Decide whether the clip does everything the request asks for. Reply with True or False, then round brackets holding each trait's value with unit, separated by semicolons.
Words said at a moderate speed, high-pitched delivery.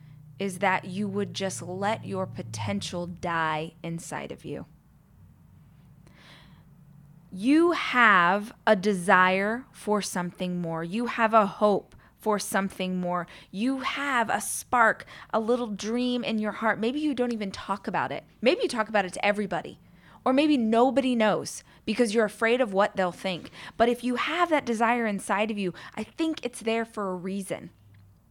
True (165 wpm; 205 Hz)